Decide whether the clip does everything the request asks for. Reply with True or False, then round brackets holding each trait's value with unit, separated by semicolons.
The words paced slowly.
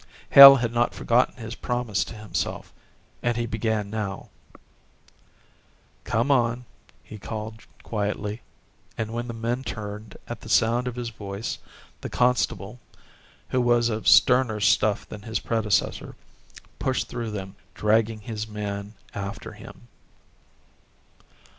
True (130 wpm)